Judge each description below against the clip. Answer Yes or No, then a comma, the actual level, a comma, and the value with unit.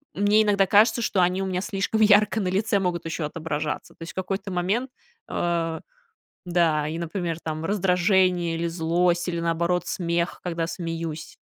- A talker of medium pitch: Yes, medium, 175 Hz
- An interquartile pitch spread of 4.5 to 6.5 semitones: No, average, 2.8 semitones